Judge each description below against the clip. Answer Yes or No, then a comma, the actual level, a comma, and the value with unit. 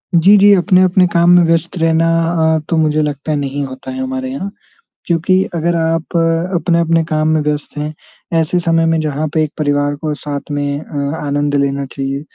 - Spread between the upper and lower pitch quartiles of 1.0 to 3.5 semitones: Yes, average, 2.8 semitones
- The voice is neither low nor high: Yes, medium, 160 Hz